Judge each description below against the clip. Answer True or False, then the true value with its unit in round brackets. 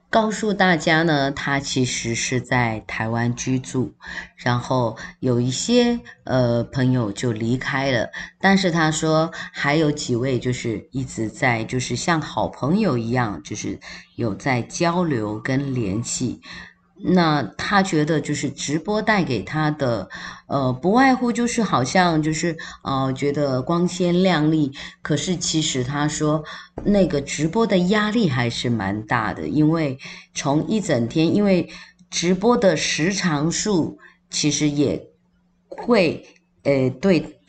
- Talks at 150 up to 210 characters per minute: True (195 characters per minute)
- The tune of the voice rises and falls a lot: True (5.8 semitones)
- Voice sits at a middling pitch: True (150 Hz)